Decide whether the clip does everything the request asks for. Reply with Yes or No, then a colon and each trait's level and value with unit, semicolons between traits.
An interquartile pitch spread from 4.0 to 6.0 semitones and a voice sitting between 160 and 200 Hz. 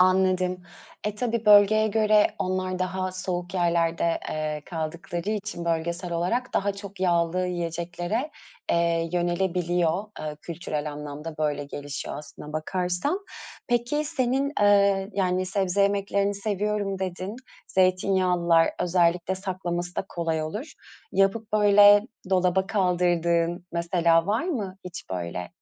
No: average, 2.9 semitones; medium, 185 Hz